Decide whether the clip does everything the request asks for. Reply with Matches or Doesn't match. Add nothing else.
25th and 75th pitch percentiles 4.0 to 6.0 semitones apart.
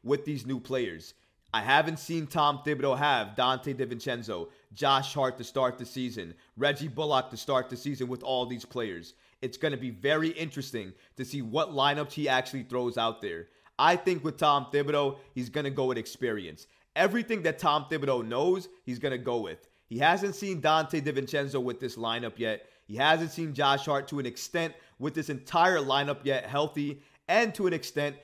Doesn't match